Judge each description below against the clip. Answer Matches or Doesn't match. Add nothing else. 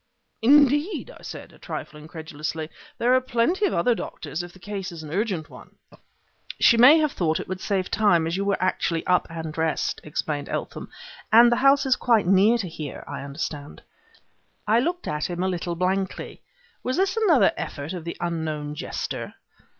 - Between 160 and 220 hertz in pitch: Matches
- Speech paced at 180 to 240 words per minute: Matches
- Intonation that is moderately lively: Doesn't match